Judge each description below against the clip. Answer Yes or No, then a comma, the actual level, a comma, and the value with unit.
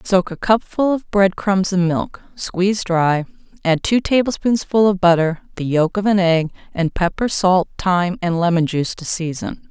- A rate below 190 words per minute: Yes, average, 180 wpm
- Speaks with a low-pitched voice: No, medium, 185 Hz